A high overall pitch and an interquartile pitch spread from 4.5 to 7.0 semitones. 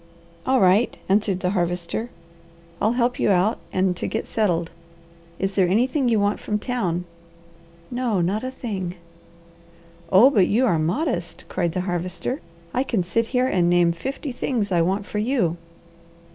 Yes: high, 200 Hz; average, 5.3 semitones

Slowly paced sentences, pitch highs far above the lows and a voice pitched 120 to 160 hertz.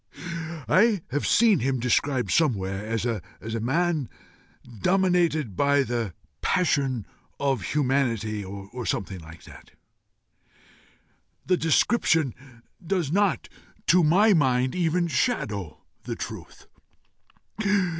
Yes: slow, 100 wpm; wide, 7.5 semitones; medium, 140 Hz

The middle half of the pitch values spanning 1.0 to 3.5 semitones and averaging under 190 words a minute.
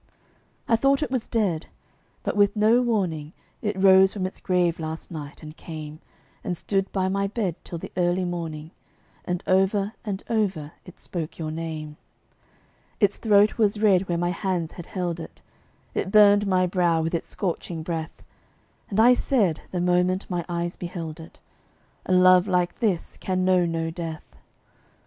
Yes: average, 3.2 semitones; average, 170 wpm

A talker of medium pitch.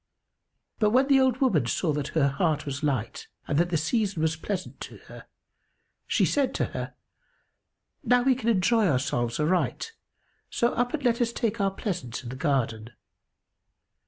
Yes: medium, 180 Hz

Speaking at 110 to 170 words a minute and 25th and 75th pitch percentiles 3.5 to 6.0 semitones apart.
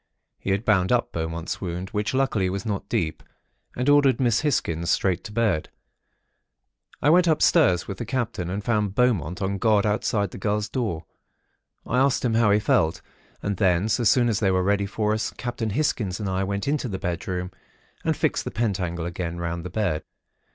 No: average, 190 wpm; average, 4.3 semitones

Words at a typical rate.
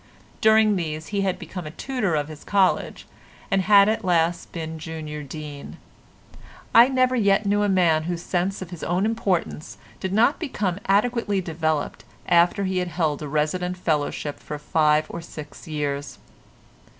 Yes: average, 160 wpm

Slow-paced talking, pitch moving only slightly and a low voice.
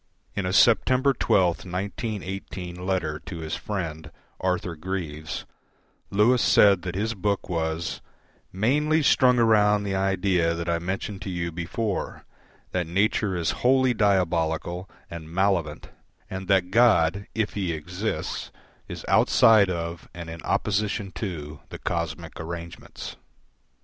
No: slow, 130 wpm; average, 3.5 semitones; very low, 95 Hz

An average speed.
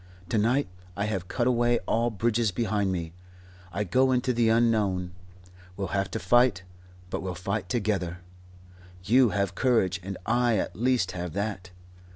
Yes: average, 160 wpm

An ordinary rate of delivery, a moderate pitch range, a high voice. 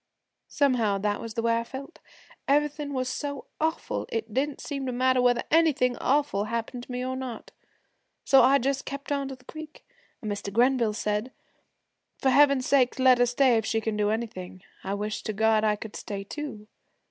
Yes: average, 195 wpm; average, 3.9 semitones; very high, 250 Hz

